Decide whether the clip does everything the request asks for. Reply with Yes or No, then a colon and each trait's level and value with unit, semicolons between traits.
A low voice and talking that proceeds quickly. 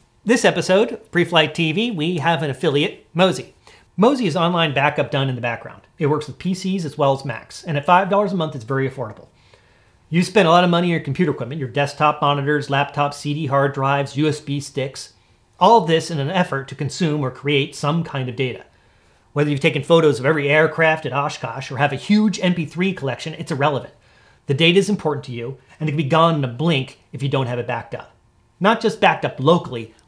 No: medium, 150 Hz; fast, 215 wpm